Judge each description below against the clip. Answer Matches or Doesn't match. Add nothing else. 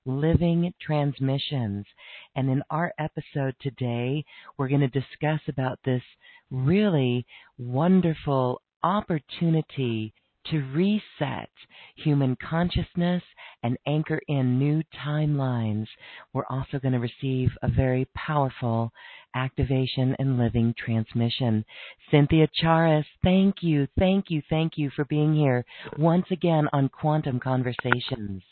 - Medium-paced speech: Doesn't match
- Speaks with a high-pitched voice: Doesn't match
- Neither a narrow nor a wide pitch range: Matches